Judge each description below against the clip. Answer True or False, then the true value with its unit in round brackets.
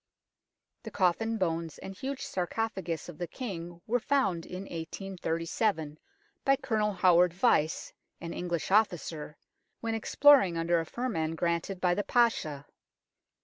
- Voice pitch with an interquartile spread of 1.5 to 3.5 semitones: False (4.9 semitones)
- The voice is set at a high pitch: False (180 Hz)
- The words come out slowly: True (130 wpm)